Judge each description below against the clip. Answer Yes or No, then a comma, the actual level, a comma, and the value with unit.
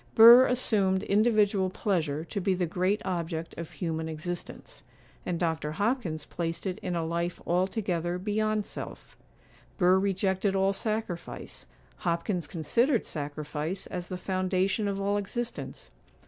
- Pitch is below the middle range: No, medium, 185 Hz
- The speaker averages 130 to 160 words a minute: Yes, slow, 135 wpm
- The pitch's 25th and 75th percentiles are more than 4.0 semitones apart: No, average, 3.2 semitones